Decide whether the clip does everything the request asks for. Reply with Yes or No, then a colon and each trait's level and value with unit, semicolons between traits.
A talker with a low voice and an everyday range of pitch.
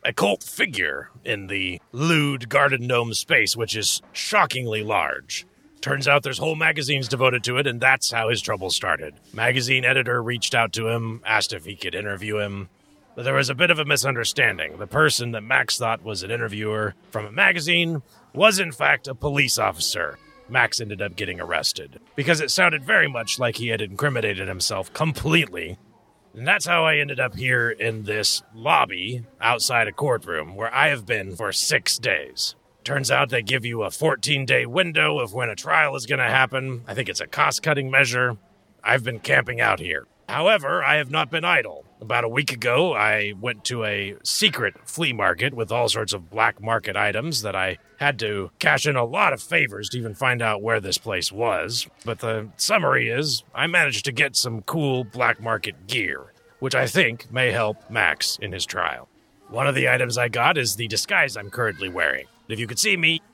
Yes: low, 120 Hz; average, 3.9 semitones